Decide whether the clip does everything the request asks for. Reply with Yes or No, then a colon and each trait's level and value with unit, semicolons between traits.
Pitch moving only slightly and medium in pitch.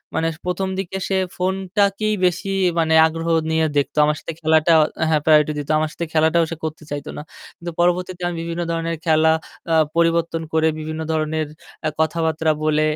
Yes: narrow, 1.8 semitones; medium, 165 Hz